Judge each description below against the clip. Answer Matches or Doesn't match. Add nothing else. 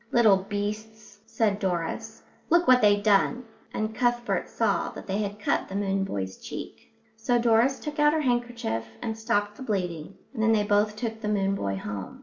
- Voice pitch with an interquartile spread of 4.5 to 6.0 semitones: Doesn't match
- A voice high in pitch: Matches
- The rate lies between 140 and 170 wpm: Doesn't match